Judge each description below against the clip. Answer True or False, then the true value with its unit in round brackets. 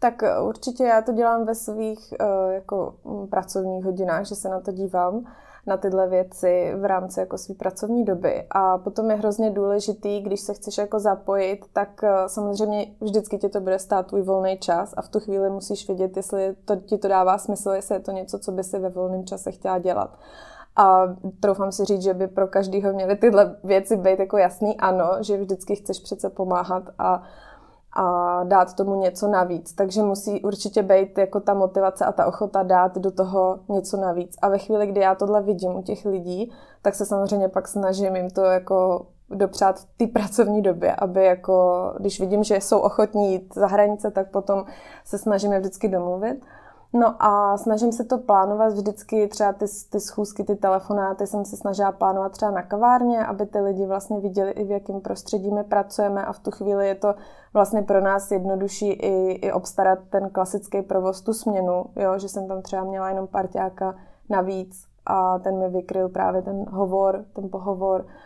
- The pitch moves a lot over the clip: False (1.5 semitones)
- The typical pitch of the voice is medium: False (195 Hz)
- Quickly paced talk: True (190 wpm)